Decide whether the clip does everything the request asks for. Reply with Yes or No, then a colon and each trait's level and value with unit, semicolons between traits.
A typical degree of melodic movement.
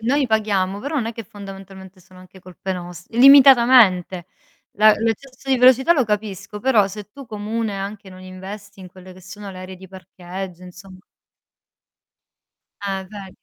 Yes: average, 3.2 semitones